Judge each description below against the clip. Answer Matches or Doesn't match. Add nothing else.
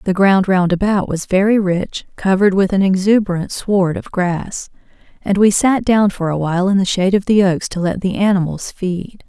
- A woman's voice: Matches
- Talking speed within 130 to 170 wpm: Doesn't match